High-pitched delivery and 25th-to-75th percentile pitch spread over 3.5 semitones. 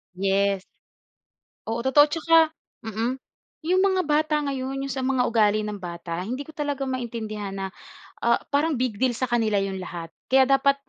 Yes: very high, 250 Hz; average, 5.2 semitones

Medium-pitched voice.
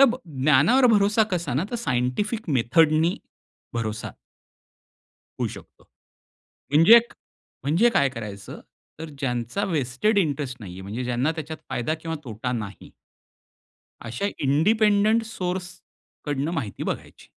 Yes: medium, 150 Hz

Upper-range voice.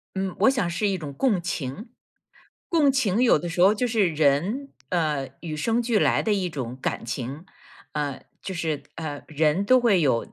No: medium, 175 Hz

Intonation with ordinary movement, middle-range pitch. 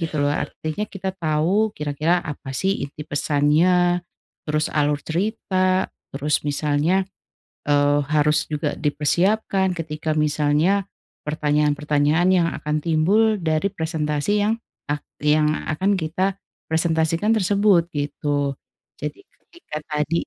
Yes: average, 3.6 semitones; medium, 155 Hz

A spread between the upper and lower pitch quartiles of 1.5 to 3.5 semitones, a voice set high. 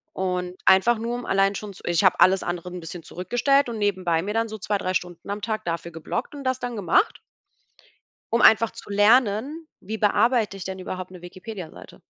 No: average, 3.9 semitones; high, 200 Hz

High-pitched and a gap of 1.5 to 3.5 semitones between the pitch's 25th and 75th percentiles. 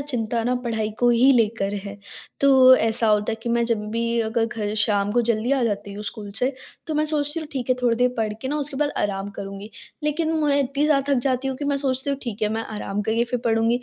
No: high, 235 Hz; average, 3.9 semitones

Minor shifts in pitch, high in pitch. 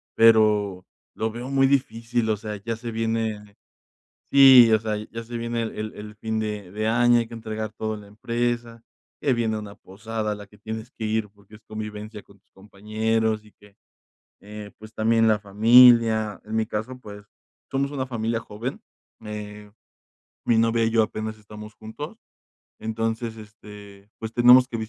No: narrow, 1.6 semitones; low, 110 Hz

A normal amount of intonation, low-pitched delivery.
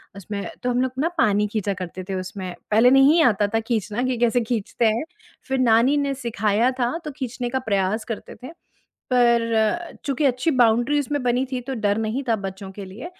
No: average, 3.6 semitones; high, 235 Hz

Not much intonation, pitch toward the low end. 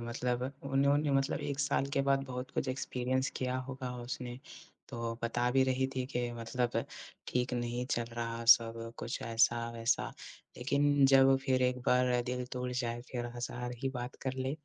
Yes: narrow, 1.7 semitones; low, 125 Hz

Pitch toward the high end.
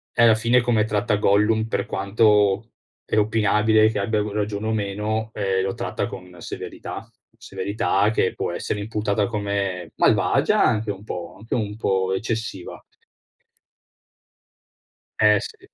No: low, 105 Hz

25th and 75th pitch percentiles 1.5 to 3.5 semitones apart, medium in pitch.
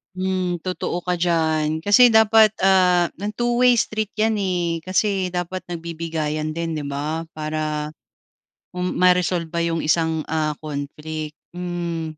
Yes: average, 2.9 semitones; medium, 170 Hz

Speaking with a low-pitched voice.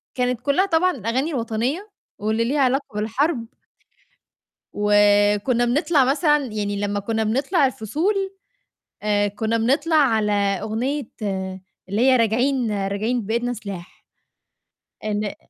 No: high, 230 Hz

